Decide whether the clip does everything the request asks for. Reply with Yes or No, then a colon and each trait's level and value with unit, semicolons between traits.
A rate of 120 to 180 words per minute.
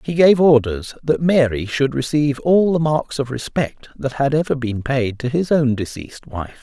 No: average, 200 wpm